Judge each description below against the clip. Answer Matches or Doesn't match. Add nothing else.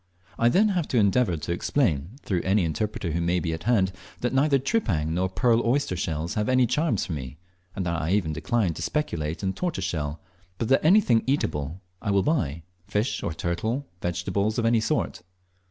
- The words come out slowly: Doesn't match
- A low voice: Matches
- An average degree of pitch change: Doesn't match